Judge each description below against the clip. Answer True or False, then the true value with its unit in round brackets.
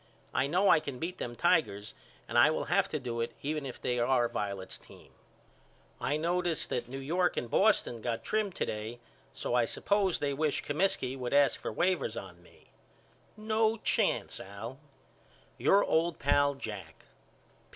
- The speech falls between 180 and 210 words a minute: False (170 wpm)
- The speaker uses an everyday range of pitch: False (6.6 semitones)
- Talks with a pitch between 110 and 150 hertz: True (140 Hz)